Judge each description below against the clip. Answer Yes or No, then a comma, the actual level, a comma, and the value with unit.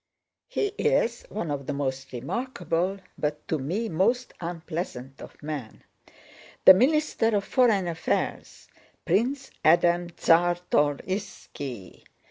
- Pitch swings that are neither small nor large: No, wide, 6.9 semitones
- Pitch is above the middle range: No, medium, 175 Hz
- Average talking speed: No, slow, 100 wpm